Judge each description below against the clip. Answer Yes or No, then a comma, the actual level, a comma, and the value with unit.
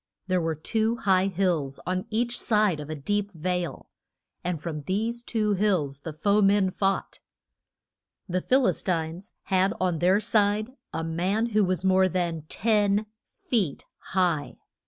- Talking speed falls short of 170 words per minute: Yes, average, 155 wpm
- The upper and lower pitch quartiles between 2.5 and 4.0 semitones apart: Yes, average, 3.7 semitones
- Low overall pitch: No, medium, 185 Hz